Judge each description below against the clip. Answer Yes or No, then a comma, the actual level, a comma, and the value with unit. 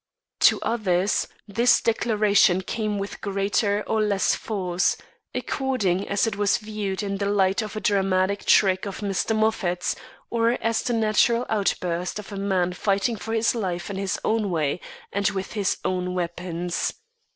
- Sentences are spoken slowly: No, average, 160 wpm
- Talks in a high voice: Yes, high, 200 Hz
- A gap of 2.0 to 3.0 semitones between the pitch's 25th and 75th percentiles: Yes, narrow, 2.5 semitones